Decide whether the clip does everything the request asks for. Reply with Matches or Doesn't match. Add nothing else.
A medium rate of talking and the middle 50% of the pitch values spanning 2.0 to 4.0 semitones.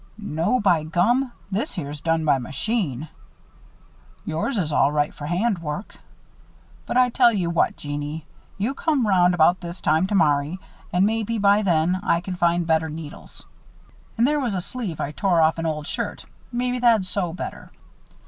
Doesn't match